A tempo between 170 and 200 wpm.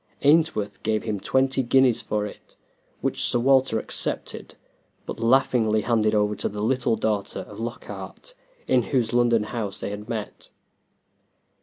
No: average, 145 wpm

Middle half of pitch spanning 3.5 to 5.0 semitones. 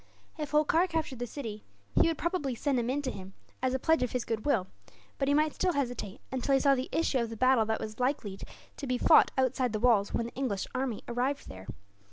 Yes: average, 3.8 semitones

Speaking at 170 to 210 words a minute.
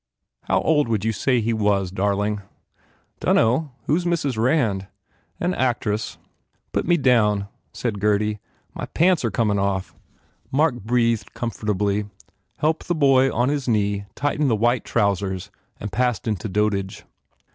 No: average, 145 wpm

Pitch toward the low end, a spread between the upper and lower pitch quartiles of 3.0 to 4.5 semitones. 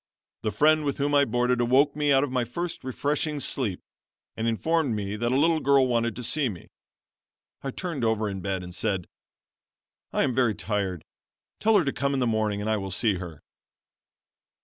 No: low, 120 Hz; average, 5.1 semitones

